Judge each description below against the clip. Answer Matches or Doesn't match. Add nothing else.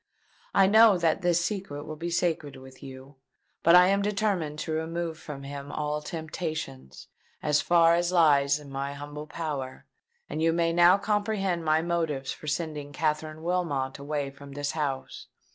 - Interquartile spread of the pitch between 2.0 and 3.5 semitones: Matches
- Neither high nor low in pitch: Matches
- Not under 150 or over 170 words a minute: Matches